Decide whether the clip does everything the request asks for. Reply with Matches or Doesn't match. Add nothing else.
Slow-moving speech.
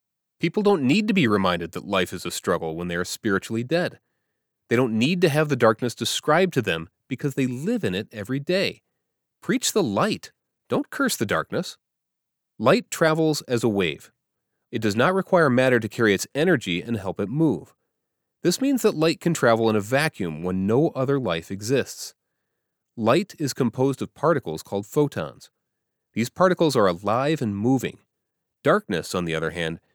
Doesn't match